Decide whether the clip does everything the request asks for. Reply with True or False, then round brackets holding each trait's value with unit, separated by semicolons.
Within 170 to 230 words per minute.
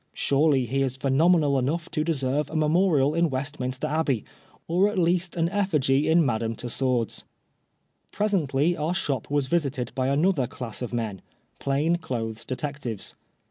False (150 wpm)